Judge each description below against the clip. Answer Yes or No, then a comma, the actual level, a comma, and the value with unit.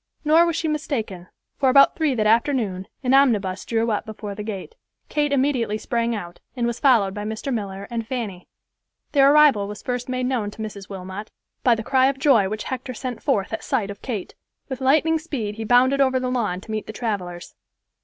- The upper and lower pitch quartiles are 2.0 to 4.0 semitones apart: No, average, 4.4 semitones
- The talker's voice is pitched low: No, high, 235 Hz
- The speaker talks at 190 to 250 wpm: Yes, fast, 205 wpm